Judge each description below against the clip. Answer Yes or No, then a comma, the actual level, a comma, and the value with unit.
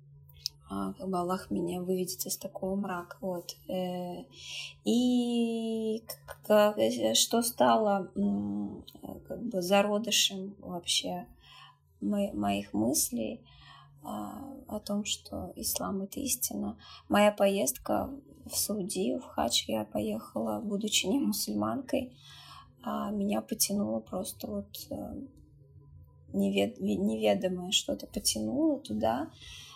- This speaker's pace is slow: Yes, slow, 90 wpm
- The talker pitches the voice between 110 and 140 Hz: No, medium, 185 Hz